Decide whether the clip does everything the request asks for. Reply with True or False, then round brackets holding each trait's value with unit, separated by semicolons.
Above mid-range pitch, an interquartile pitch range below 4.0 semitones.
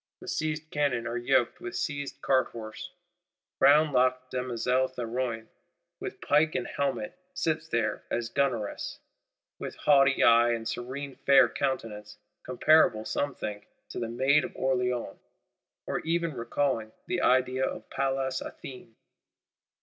False (130 Hz; 3.1 semitones)